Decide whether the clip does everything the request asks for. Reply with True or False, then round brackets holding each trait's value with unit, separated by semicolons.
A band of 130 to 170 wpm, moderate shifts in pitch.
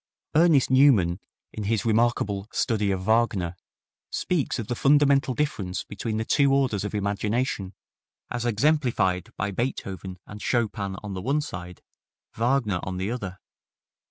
True (140 wpm; 5.0 semitones)